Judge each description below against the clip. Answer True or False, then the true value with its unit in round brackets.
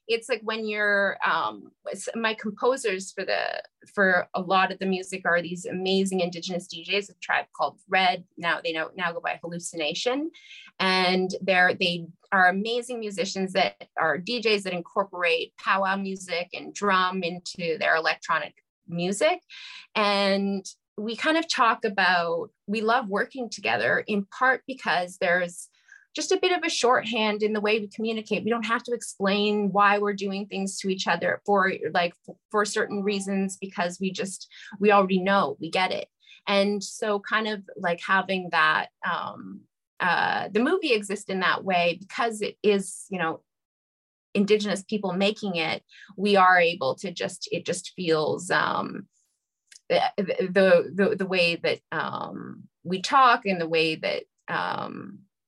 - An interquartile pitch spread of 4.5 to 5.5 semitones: False (3.0 semitones)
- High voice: True (195 Hz)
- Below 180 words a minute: True (160 wpm)